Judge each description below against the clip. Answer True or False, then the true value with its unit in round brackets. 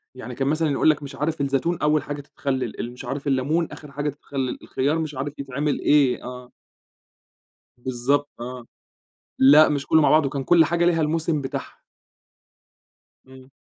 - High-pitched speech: False (140 Hz)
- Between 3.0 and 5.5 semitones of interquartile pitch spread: False (2.6 semitones)